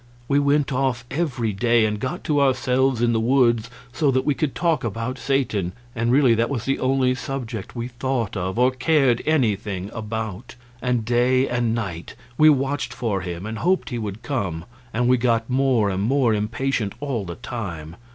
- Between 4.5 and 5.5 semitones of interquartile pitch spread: No, average, 3.5 semitones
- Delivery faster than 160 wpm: Yes, average, 185 wpm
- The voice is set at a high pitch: No, low, 120 Hz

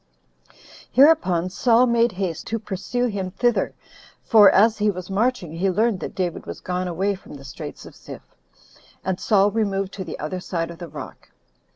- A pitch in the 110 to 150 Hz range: No, high, 195 Hz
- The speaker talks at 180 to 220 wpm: Yes, average, 185 wpm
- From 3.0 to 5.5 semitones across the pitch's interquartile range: Yes, average, 3.7 semitones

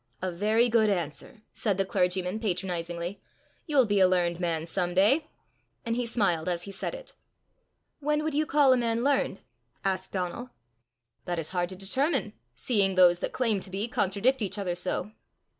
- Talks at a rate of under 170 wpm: No, average, 175 wpm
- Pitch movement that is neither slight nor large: Yes, average, 5.0 semitones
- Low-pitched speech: No, high, 195 Hz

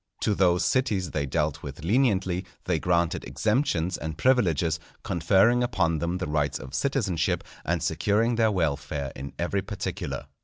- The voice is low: Yes, very low, 90 Hz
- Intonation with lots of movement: No, average, 4.6 semitones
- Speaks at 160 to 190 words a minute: No, average, 150 wpm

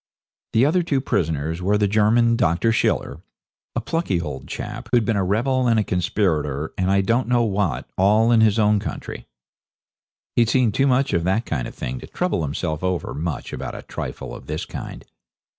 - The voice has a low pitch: Yes, low, 105 Hz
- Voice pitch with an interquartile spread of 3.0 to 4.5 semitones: No, wide, 5.4 semitones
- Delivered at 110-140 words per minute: No, average, 195 wpm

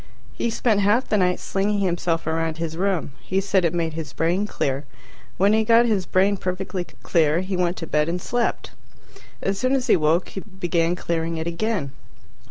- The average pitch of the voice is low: No, medium, 180 Hz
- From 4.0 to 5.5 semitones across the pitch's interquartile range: No, average, 3.5 semitones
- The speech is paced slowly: No, average, 190 wpm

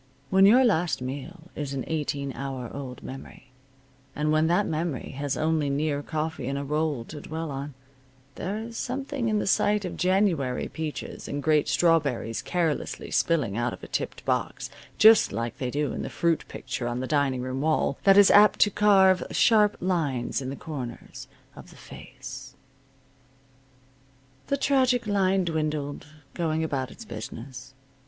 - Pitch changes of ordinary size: No, wide, 5.7 semitones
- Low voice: No, medium, 155 Hz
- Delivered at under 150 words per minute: No, average, 165 wpm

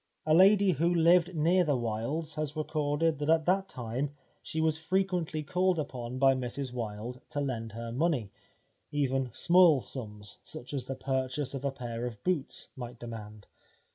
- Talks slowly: No, average, 170 wpm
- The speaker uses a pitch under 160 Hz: Yes, medium, 140 Hz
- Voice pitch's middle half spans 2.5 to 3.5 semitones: No, average, 4.8 semitones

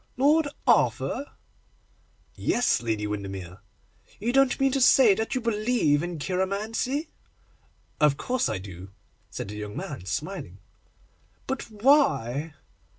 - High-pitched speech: Yes, high, 195 Hz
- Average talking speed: No, slow, 120 wpm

